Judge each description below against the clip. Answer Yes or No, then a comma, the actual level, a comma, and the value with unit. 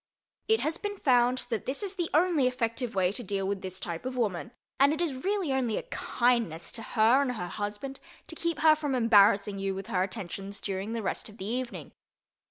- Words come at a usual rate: No, fast, 215 wpm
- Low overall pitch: No, high, 235 Hz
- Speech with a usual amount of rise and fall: No, wide, 5.9 semitones